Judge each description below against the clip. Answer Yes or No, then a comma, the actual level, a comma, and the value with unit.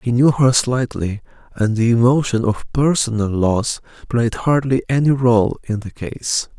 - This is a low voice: Yes, low, 120 Hz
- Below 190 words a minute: Yes, average, 155 wpm